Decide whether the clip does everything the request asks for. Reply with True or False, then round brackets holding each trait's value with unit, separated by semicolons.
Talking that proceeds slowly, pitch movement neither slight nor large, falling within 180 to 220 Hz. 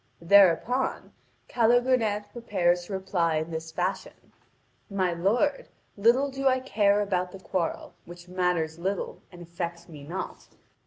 True (130 wpm; 4.3 semitones; 190 Hz)